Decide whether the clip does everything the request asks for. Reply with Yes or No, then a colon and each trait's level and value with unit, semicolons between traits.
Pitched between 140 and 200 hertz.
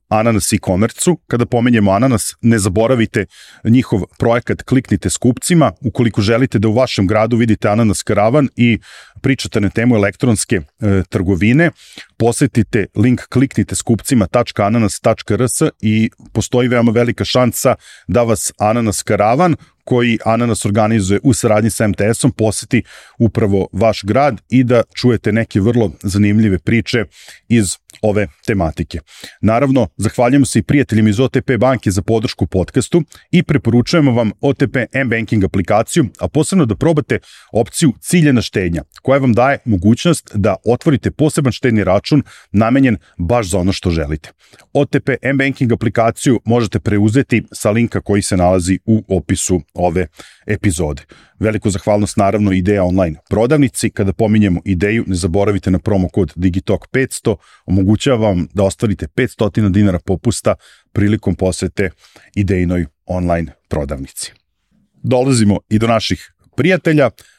No: low, 110 Hz